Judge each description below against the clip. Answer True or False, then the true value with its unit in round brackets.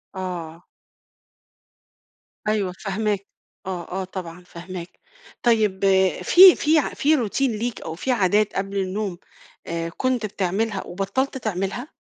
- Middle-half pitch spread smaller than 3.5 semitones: False (3.8 semitones)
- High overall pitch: True (195 Hz)